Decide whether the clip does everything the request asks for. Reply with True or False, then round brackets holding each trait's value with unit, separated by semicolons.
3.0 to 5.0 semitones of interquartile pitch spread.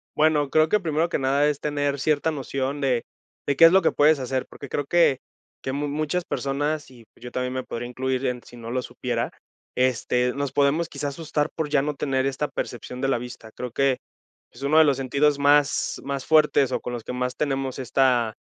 False (2.6 semitones)